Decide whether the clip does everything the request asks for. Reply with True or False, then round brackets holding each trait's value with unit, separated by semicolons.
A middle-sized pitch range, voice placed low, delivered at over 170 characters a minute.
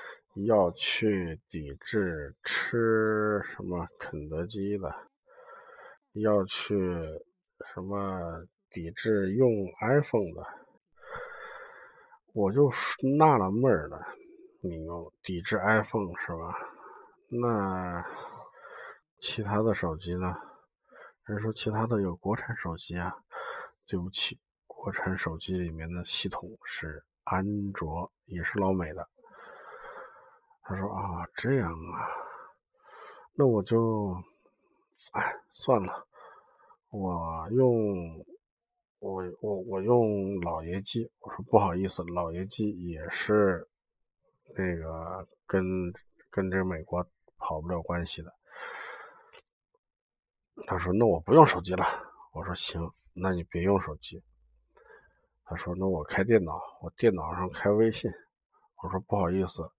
False (4.7 semitones; 95 Hz; 165 characters per minute)